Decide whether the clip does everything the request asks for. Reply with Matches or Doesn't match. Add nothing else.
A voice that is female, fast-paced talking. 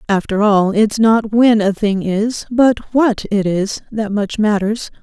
Doesn't match